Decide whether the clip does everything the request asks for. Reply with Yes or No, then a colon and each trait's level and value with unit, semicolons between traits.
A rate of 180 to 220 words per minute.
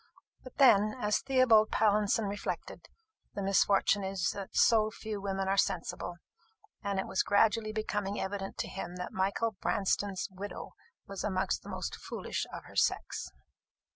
No: average, 150 wpm